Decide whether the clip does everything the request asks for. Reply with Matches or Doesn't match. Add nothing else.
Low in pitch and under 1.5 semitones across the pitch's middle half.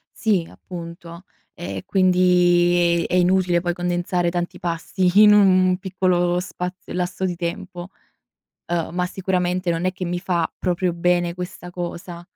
Doesn't match